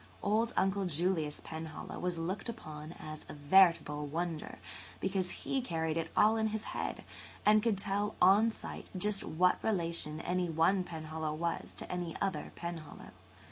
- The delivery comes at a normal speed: Yes, average, 155 wpm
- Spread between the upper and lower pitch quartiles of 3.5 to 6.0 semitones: Yes, average, 3.8 semitones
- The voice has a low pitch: No, medium, 175 Hz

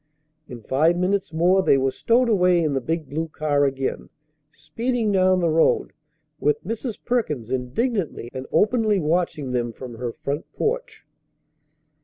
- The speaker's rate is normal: Yes, average, 150 wpm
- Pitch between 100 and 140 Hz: No, medium, 165 Hz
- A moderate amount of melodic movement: No, wide, 6.9 semitones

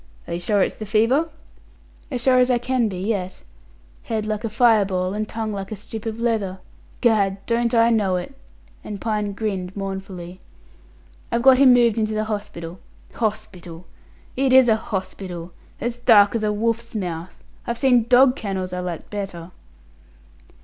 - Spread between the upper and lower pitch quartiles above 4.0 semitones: No, average, 3.4 semitones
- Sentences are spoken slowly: No, average, 170 wpm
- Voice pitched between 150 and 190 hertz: No, high, 215 Hz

